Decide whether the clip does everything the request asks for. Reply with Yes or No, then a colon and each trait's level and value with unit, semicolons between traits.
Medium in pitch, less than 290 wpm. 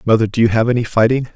No: low, 115 Hz; fast, 265 wpm